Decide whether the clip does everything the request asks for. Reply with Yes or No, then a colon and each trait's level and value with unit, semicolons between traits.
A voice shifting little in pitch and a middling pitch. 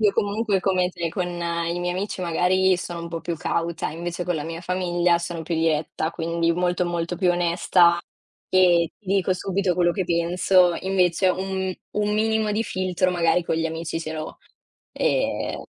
Yes: narrow, 1.8 semitones; medium, 175 Hz